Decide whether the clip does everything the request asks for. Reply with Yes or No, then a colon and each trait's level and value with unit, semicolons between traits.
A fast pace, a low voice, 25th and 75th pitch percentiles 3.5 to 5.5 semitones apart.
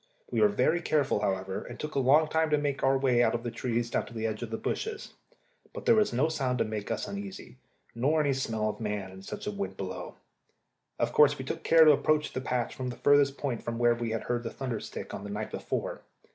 Yes: fast, 255 wpm; low, 125 Hz; average, 5.0 semitones